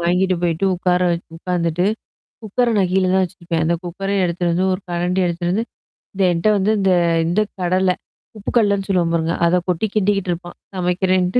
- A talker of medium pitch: Yes, medium, 180 Hz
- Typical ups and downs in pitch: No, narrow, 1.8 semitones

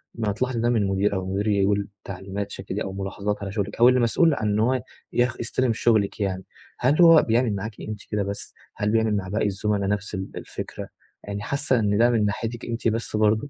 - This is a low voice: Yes, low, 105 Hz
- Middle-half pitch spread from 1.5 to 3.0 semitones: Yes, average, 2.7 semitones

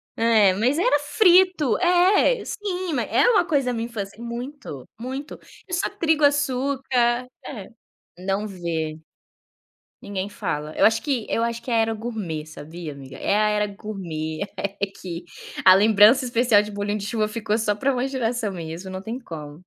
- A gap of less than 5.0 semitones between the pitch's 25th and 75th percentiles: No, wide, 5.6 semitones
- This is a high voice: Yes, high, 225 Hz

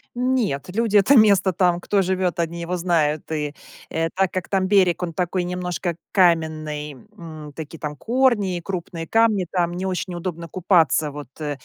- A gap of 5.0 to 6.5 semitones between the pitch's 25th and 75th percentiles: No, average, 2.9 semitones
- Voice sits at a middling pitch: Yes, medium, 175 Hz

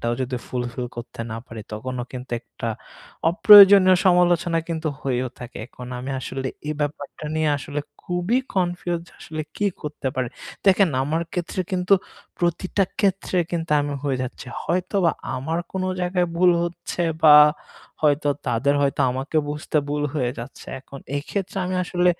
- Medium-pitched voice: Yes, medium, 155 Hz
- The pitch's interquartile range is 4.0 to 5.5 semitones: Yes, average, 5.2 semitones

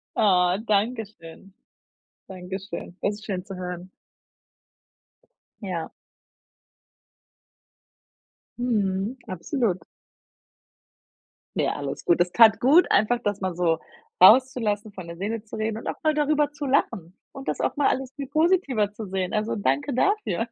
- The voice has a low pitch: No, high, 205 Hz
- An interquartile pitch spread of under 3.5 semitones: No, average, 5.3 semitones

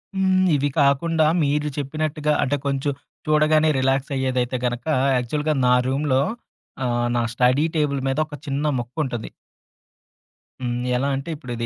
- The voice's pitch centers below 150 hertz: Yes, medium, 140 Hz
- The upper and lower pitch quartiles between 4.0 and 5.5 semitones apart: No, average, 2.9 semitones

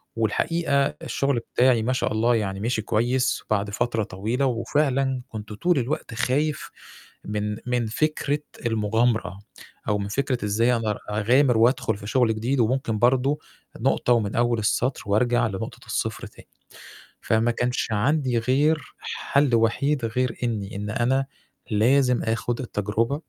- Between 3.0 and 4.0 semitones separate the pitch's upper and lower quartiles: Yes, average, 3.3 semitones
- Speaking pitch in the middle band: No, low, 120 Hz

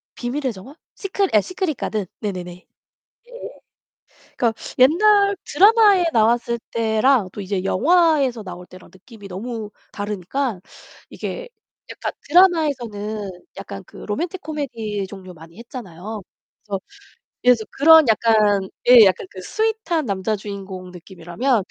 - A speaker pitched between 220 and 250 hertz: Yes, high, 225 Hz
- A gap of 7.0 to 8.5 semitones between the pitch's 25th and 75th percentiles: Yes, wide, 7.3 semitones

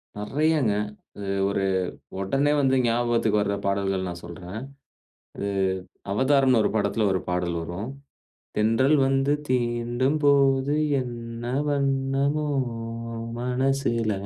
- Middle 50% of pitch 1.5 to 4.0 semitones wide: No, average, 4.8 semitones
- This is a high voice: No, low, 120 Hz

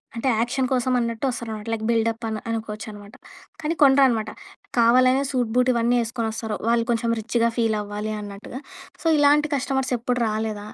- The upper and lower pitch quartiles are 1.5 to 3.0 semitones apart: Yes, narrow, 2.4 semitones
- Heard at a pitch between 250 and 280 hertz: No, high, 230 Hz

